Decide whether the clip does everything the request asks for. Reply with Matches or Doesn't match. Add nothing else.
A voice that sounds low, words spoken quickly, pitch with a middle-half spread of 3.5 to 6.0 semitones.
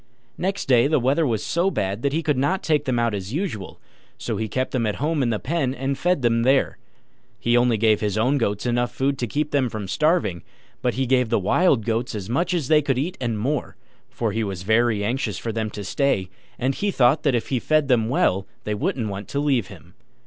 Matches